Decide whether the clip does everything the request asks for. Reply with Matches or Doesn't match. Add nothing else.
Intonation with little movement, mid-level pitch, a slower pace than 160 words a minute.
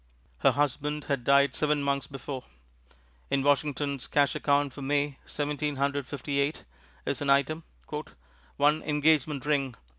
Matches